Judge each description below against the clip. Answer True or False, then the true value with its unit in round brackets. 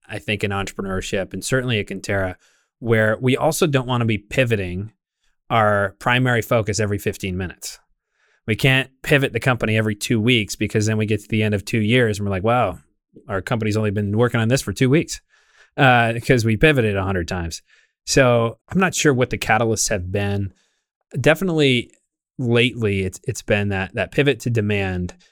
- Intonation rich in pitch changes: False (3.9 semitones)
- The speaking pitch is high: False (110 Hz)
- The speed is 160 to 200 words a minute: True (190 wpm)